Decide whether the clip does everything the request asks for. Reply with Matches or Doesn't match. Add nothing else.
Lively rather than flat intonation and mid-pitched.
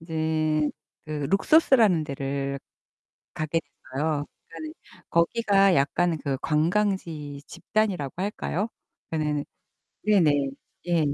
Doesn't match